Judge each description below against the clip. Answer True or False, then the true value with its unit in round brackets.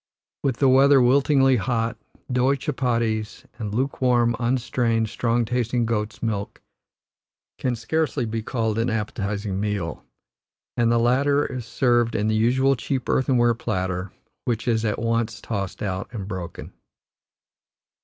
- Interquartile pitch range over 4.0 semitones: False (2.6 semitones)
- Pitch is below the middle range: True (115 Hz)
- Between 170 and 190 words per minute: False (135 wpm)